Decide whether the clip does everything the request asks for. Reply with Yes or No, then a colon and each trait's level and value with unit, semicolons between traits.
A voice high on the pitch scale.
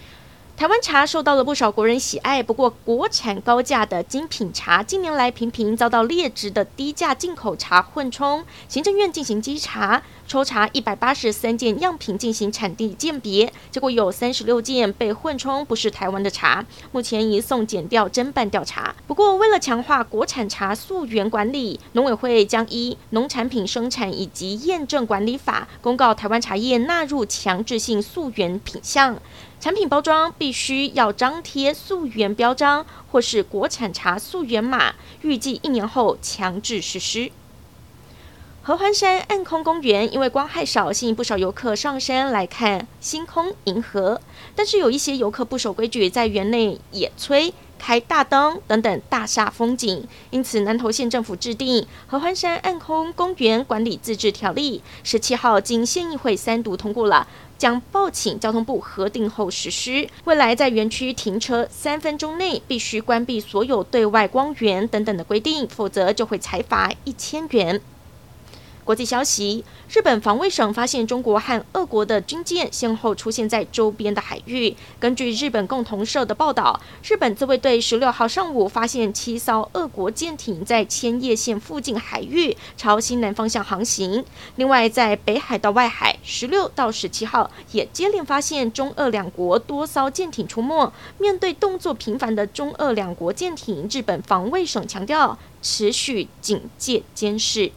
Yes: high, 235 Hz